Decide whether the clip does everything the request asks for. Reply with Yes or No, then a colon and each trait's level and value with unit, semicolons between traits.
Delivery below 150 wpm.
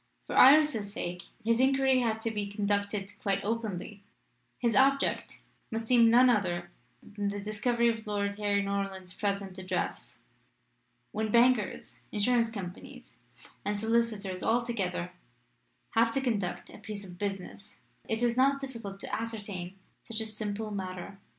Yes: average, 140 wpm